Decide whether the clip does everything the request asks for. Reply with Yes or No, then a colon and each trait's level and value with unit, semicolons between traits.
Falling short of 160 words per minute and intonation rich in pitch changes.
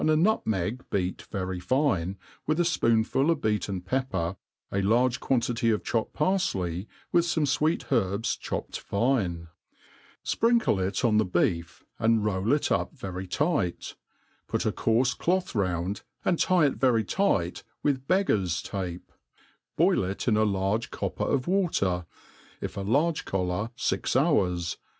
Yes: average, 145 wpm; wide, 7.2 semitones